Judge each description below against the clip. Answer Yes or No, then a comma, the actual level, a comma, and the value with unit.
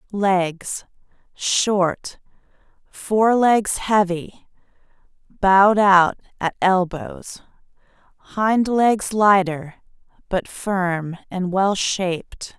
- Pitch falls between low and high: No, high, 195 Hz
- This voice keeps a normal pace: No, slow, 75 wpm